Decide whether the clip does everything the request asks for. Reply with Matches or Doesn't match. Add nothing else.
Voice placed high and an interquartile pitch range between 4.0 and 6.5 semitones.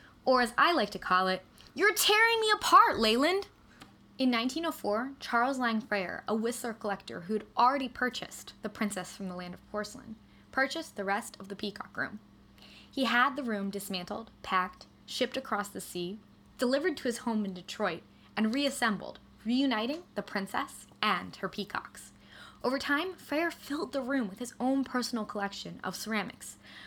Matches